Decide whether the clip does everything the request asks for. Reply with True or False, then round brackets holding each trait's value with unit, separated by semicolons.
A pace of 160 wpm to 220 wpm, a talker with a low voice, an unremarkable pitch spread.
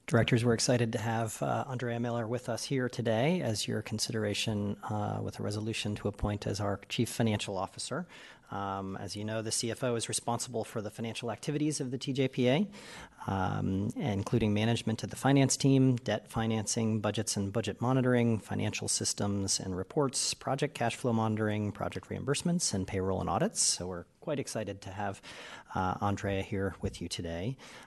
True (170 wpm; 110 Hz; 3.1 semitones)